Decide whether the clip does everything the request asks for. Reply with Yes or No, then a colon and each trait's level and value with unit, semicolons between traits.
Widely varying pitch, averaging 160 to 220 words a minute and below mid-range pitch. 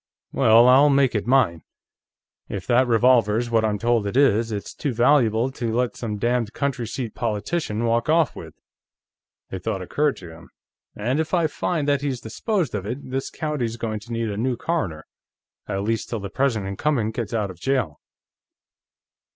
No: average, 4.1 semitones; average, 180 wpm; low, 120 Hz